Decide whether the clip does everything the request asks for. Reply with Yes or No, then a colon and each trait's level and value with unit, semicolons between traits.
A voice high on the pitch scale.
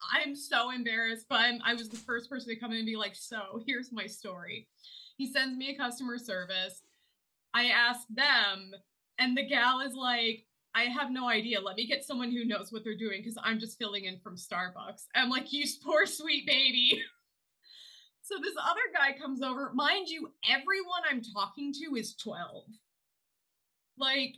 Yes: high, 245 Hz